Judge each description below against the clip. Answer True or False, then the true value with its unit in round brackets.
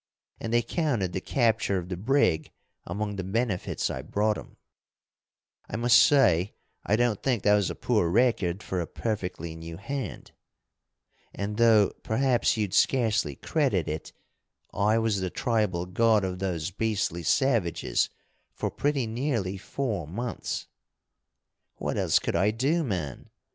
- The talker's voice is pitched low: True (105 Hz)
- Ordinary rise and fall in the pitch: True (4.4 semitones)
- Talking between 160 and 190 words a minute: False (145 wpm)